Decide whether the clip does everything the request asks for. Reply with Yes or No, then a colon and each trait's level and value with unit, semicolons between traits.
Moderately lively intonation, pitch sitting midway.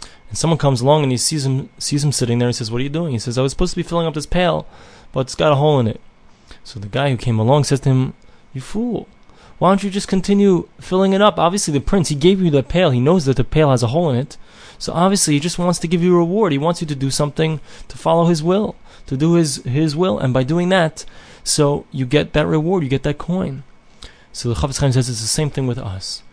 Yes: average, 4.7 semitones; medium, 150 Hz